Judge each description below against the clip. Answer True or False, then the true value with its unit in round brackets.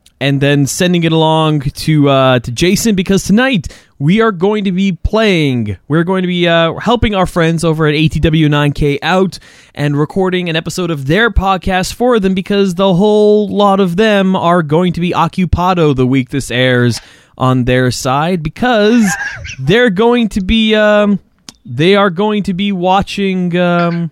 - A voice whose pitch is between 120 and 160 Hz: False (175 Hz)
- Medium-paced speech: True (170 wpm)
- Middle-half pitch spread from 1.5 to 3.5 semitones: False (4.9 semitones)